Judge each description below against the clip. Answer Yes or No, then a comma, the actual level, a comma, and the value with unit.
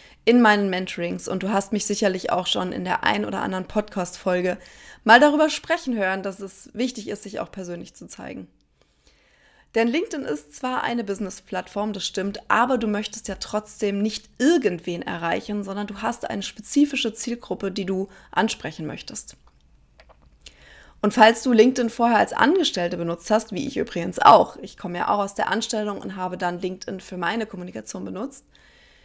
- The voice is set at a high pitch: Yes, high, 205 Hz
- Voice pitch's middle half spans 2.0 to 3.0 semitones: No, average, 3.5 semitones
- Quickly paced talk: No, average, 170 wpm